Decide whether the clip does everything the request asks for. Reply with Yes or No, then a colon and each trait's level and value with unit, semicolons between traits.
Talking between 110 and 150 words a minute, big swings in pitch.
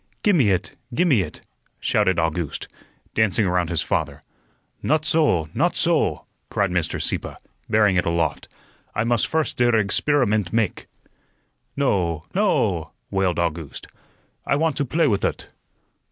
Yes: average, 140 wpm; wide, 7.8 semitones